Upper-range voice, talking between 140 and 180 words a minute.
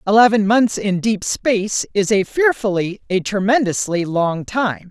Yes: high, 205 Hz; average, 145 wpm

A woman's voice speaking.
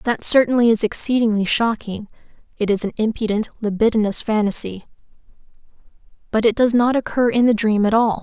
Yes: female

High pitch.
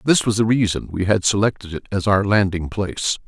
No: low, 100 Hz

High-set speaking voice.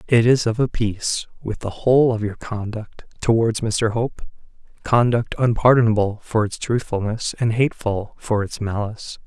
No: low, 110 Hz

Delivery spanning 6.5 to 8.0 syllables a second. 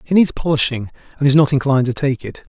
Yes: 6.6 syllables/s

